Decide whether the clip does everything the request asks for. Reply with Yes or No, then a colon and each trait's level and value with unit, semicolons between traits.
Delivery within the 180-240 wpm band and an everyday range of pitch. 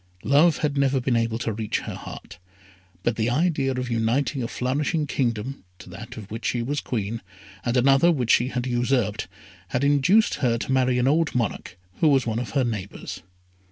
Yes: average, 190 wpm; average, 3.2 semitones